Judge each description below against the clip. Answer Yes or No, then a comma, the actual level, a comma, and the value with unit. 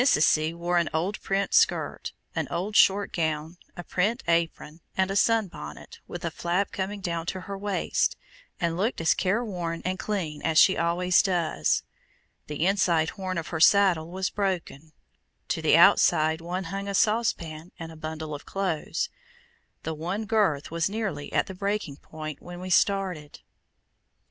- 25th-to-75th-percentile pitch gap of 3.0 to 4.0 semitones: Yes, average, 3.5 semitones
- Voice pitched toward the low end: No, medium, 175 Hz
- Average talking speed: Yes, average, 165 wpm